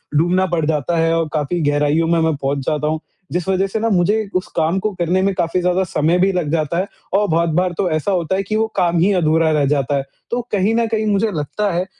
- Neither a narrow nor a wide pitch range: Yes, average, 3.4 semitones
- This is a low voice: No, medium, 175 Hz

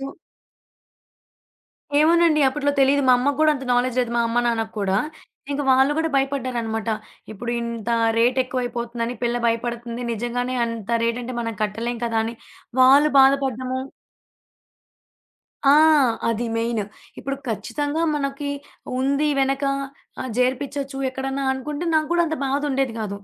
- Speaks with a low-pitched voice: No, very high, 255 Hz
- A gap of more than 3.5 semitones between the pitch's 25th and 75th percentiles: No, average, 2.9 semitones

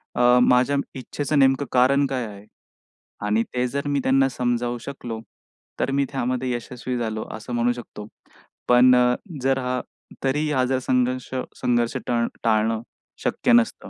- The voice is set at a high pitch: No, low, 125 Hz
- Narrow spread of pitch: Yes, narrow, 1.9 semitones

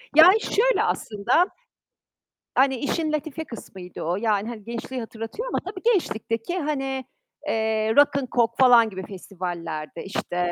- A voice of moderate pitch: No, high, 235 Hz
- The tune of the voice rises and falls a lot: Yes, wide, 6.2 semitones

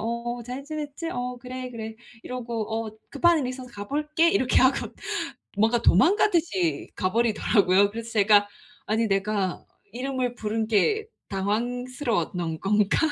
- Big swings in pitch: No, average, 3.6 semitones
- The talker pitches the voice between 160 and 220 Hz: No, high, 235 Hz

